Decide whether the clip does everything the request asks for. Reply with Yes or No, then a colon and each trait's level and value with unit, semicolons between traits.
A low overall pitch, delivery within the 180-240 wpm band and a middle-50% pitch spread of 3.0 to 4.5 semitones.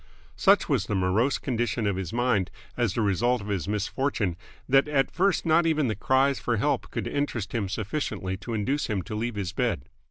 No: low, 115 Hz; average, 200 wpm; average, 5.2 semitones